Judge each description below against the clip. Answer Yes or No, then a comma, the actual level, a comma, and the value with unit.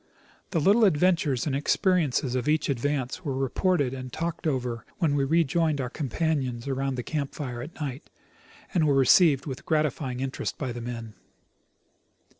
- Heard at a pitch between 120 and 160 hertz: Yes, medium, 140 Hz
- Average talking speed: Yes, average, 160 wpm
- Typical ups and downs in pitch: Yes, average, 3.6 semitones